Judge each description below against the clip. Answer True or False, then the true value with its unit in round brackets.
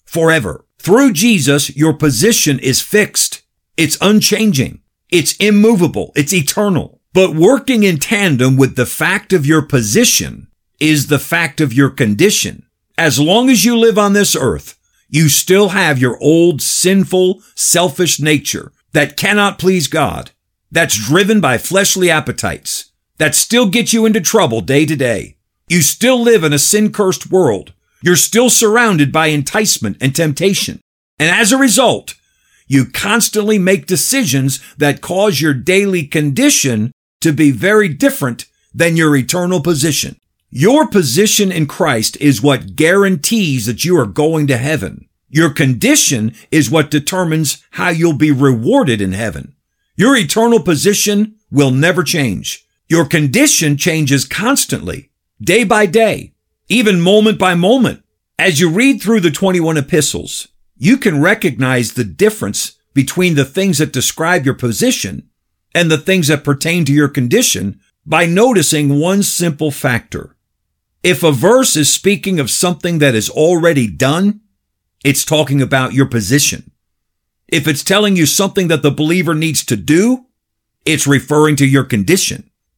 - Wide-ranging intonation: True (5.8 semitones)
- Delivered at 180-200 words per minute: False (150 wpm)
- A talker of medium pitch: True (165 Hz)